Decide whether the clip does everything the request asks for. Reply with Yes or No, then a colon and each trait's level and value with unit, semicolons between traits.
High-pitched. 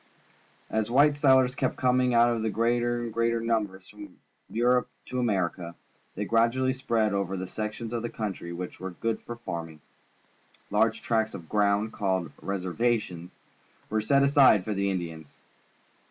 No: low, 110 Hz